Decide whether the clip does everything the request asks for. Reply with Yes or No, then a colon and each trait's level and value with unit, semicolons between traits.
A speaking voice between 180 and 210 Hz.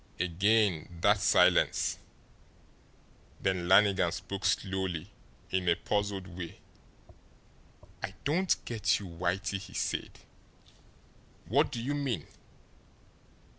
No: very low, 95 Hz